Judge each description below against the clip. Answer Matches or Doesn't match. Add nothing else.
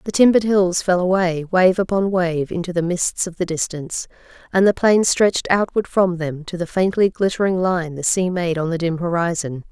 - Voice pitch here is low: Doesn't match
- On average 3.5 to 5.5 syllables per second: Matches